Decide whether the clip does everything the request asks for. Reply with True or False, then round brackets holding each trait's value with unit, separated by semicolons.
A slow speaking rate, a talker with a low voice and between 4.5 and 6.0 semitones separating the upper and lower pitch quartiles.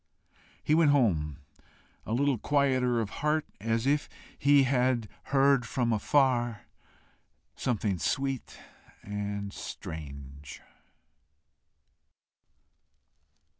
True (85 wpm; 120 Hz; 5.2 semitones)